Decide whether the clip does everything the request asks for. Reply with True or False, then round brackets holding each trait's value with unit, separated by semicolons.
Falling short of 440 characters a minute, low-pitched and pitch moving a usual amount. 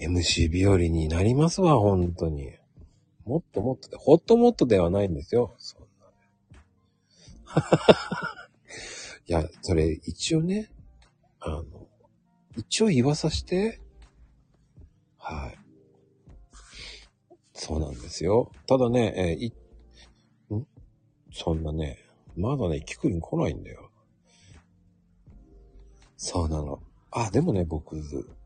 False (200 characters per minute; 90 Hz; 7.0 semitones)